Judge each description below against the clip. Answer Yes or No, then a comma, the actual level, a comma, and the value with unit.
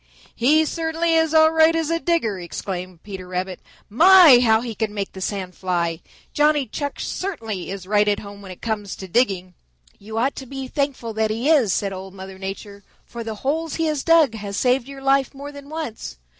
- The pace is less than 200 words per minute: No, fast, 205 wpm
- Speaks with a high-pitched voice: Yes, high, 230 Hz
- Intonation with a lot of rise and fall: Yes, wide, 7.0 semitones